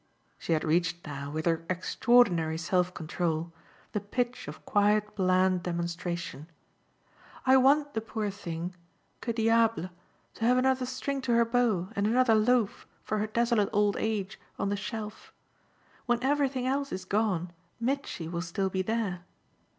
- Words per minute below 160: Yes, average, 150 wpm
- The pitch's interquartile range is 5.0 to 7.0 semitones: Yes, average, 5.3 semitones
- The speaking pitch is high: Yes, high, 205 Hz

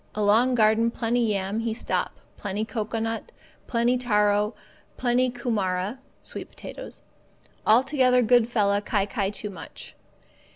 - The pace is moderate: No, slow, 120 wpm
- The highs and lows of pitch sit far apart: No, average, 2.8 semitones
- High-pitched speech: Yes, high, 225 Hz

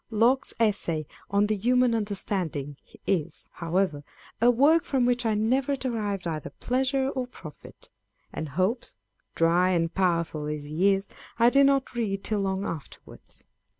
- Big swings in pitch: Yes, wide, 6.5 semitones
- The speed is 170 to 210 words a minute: No, average, 150 wpm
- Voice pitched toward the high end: Yes, high, 205 Hz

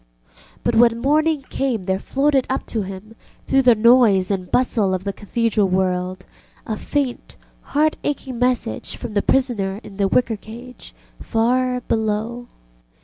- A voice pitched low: No, high, 230 Hz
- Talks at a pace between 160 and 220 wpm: No, average, 145 wpm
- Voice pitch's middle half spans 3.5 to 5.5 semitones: Yes, average, 4.3 semitones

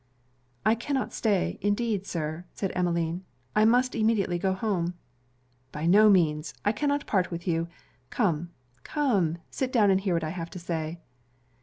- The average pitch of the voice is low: No, high, 190 Hz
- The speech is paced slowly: No, average, 160 wpm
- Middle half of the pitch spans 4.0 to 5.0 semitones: Yes, average, 4.3 semitones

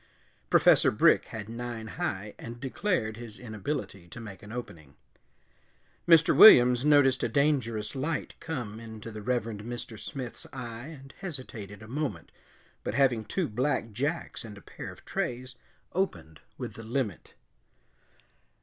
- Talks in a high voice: No, low, 120 Hz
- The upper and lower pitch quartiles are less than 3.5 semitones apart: No, average, 4.1 semitones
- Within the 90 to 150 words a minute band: Yes, average, 140 wpm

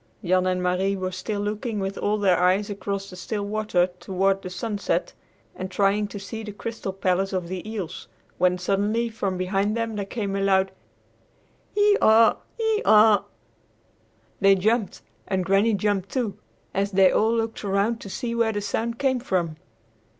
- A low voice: No, high, 200 Hz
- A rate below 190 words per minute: Yes, average, 170 wpm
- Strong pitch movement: No, narrow, 2.5 semitones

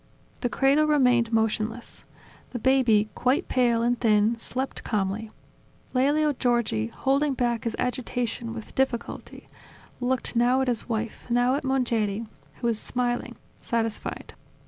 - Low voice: No, high, 240 Hz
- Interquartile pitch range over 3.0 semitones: No, narrow, 2.4 semitones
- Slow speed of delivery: Yes, slow, 130 wpm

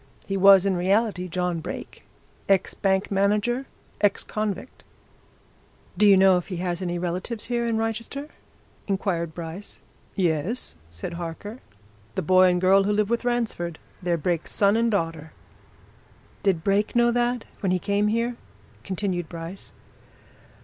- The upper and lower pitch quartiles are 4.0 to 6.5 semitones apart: No, average, 3.4 semitones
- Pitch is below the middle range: No, high, 195 Hz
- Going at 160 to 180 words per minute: No, average, 145 wpm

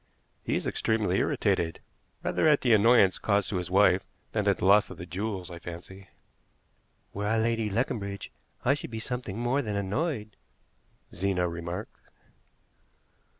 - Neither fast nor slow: Yes, average, 150 wpm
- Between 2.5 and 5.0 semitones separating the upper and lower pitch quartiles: Yes, average, 3.5 semitones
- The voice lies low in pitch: Yes, low, 100 Hz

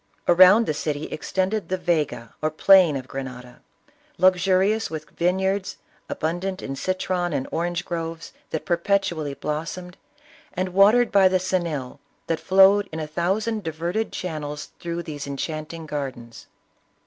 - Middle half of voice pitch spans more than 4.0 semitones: No, average, 3.5 semitones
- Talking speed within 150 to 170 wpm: No, slow, 135 wpm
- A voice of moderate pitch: Yes, medium, 170 Hz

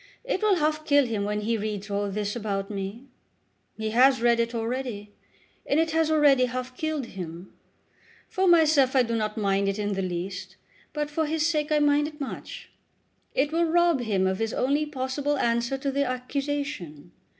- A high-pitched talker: Yes, very high, 255 Hz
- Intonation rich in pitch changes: Yes, wide, 6.1 semitones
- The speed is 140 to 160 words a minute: No, average, 185 wpm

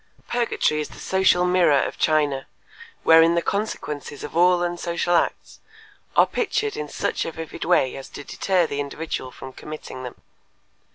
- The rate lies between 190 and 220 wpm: No, average, 160 wpm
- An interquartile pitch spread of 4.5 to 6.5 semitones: No, average, 3.6 semitones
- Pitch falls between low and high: Yes, medium, 165 Hz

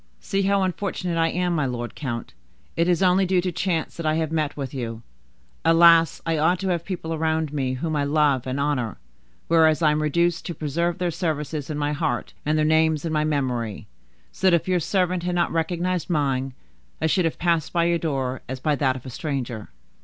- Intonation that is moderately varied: Yes, average, 3.3 semitones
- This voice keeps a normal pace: No, fast, 215 wpm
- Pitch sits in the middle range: Yes, medium, 160 Hz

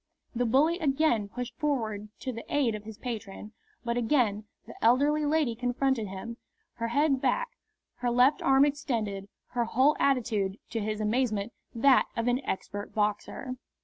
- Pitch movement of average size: Yes, average, 4.1 semitones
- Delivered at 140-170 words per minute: Yes, average, 155 wpm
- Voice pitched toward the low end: No, high, 240 Hz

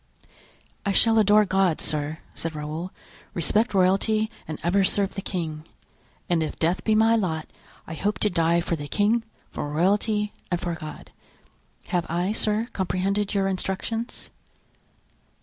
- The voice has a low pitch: No, high, 190 Hz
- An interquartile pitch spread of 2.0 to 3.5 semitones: No, average, 4.0 semitones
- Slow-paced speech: No, average, 150 wpm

